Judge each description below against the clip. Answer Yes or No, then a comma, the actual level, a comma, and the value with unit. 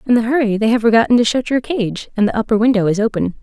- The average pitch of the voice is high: Yes, high, 225 Hz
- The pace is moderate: No, fast, 280 wpm